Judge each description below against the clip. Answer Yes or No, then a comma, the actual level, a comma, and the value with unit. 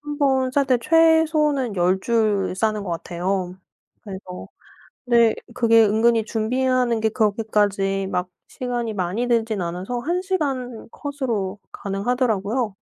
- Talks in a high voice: Yes, high, 225 Hz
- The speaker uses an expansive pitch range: No, average, 4.5 semitones